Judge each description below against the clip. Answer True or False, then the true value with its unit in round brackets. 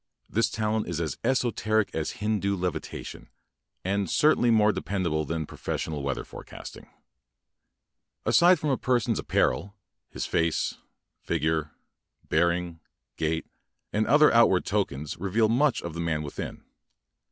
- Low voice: True (95 Hz)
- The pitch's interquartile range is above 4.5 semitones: True (5.5 semitones)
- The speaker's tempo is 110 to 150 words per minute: True (145 wpm)